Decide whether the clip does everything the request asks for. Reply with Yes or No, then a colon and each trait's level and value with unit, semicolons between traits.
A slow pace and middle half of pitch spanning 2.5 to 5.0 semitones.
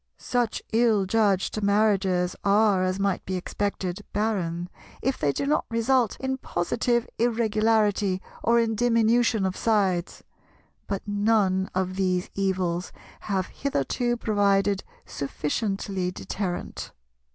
Yes: slow, 115 wpm; average, 3.3 semitones